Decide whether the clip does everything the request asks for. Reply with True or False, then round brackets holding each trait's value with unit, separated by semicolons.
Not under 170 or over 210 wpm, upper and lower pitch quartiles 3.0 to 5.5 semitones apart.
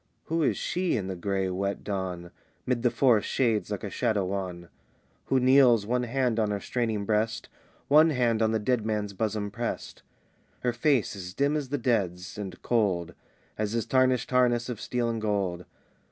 True (180 wpm; 3.9 semitones)